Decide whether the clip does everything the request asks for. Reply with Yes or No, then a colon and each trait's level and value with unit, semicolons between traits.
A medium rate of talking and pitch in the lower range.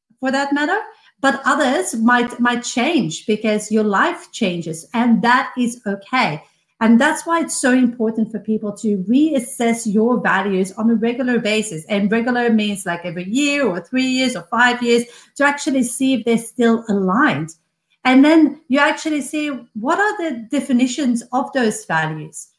No: average, 165 wpm; high, 240 Hz